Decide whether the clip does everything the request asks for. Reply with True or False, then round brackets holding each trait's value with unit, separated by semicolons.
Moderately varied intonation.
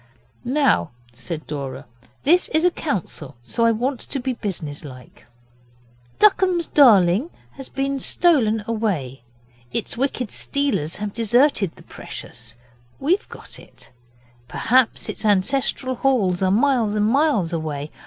False (7.7 semitones)